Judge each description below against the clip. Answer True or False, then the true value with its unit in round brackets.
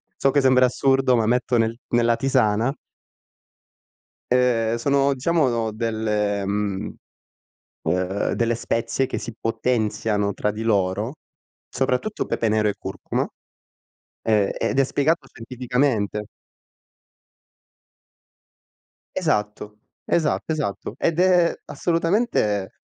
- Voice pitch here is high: False (115 Hz)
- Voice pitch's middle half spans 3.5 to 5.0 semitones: True (4.1 semitones)